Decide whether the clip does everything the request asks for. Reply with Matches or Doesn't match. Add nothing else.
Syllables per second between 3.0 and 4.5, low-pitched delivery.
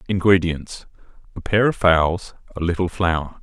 Matches